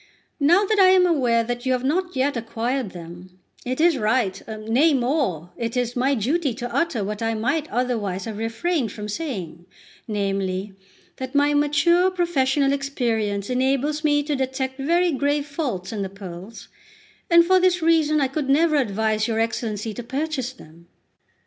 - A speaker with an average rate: Yes, average, 165 wpm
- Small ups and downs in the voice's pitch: No, wide, 5.5 semitones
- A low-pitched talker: No, very high, 260 Hz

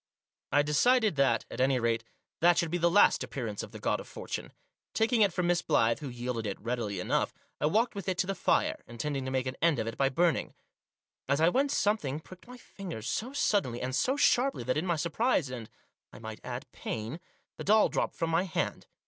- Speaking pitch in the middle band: Yes, medium, 155 Hz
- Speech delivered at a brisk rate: Yes, fast, 220 wpm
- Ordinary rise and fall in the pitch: No, wide, 7.7 semitones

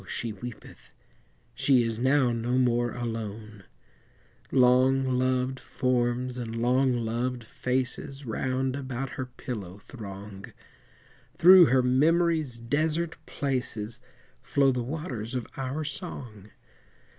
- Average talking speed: No, slow, 110 wpm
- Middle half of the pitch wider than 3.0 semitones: No, narrow, 2.4 semitones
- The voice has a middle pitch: No, low, 125 Hz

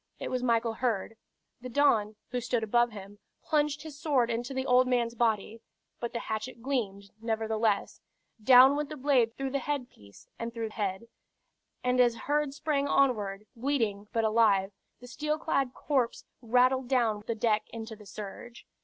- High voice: Yes, high, 240 Hz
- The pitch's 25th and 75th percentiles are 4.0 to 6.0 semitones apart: No, average, 3.2 semitones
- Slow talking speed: No, average, 160 wpm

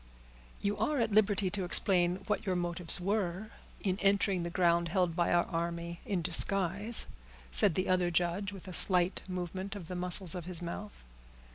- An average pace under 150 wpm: No, average, 175 wpm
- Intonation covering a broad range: No, narrow, 2.4 semitones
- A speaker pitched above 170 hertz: Yes, medium, 185 Hz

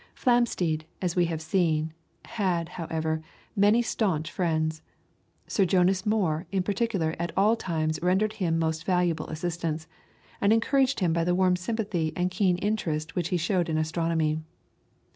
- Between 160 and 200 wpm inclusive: No, average, 150 wpm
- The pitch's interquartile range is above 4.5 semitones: No, average, 3.4 semitones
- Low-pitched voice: No, medium, 175 Hz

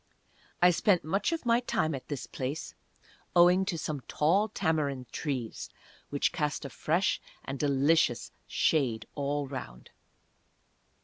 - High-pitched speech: No, medium, 150 Hz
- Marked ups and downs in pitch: No, average, 4.3 semitones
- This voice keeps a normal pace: No, slow, 130 wpm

